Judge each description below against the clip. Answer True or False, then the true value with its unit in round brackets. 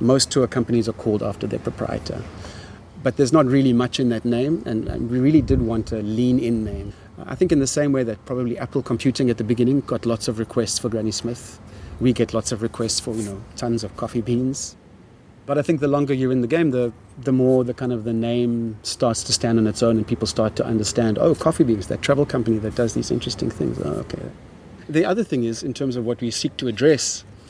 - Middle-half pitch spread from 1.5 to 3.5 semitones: True (2.8 semitones)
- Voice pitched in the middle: False (120 Hz)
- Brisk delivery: True (240 wpm)